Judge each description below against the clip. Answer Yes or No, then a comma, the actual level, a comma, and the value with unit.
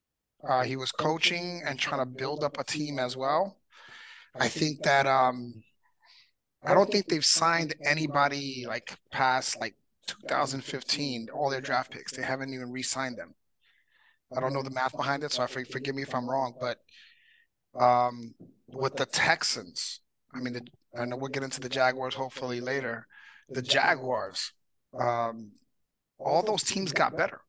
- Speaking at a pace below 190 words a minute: Yes, average, 160 wpm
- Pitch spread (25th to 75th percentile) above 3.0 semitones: No, narrow, 2.6 semitones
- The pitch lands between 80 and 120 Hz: No, low, 135 Hz